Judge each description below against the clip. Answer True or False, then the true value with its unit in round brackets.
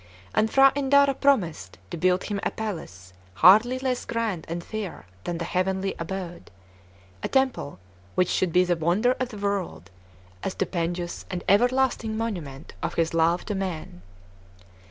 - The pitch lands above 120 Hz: True (190 Hz)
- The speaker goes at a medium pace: True (155 wpm)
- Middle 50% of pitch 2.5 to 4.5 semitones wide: False (5.1 semitones)